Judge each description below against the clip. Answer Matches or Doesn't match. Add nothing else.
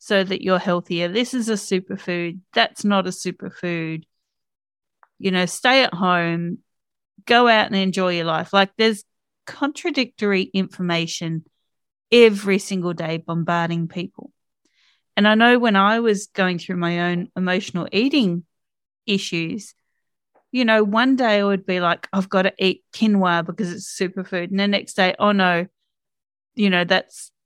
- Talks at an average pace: Matches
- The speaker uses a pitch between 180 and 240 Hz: Matches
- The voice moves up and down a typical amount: Matches